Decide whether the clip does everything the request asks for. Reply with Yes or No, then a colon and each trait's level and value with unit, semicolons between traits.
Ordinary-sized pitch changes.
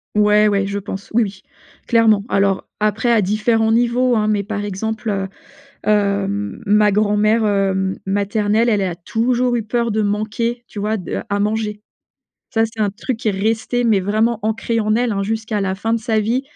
No: narrow, 2.0 semitones